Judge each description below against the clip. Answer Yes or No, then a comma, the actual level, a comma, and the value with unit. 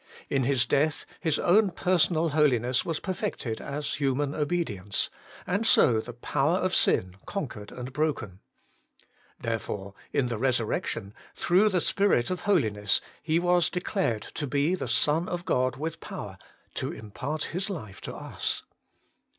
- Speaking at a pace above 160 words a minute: No, average, 145 wpm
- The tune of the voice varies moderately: No, wide, 6.5 semitones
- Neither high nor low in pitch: Yes, medium, 145 Hz